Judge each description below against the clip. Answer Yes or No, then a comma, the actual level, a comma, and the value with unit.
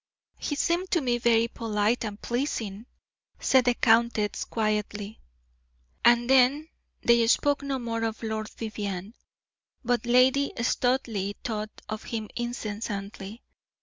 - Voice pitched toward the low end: No, high, 230 Hz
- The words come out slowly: Yes, slow, 120 wpm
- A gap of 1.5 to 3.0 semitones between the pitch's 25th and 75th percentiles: Yes, narrow, 2.6 semitones